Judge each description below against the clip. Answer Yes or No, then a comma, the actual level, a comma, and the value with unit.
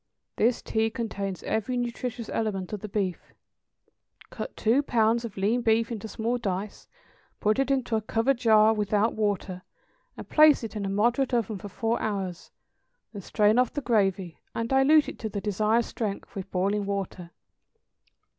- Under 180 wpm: Yes, average, 170 wpm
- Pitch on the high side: Yes, high, 220 Hz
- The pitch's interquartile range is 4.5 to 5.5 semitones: No, average, 2.9 semitones